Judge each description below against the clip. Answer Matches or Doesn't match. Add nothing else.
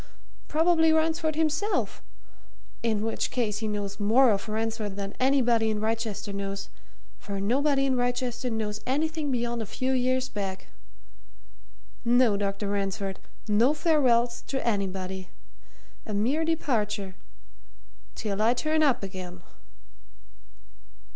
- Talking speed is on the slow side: Matches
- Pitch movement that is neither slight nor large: Matches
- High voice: Matches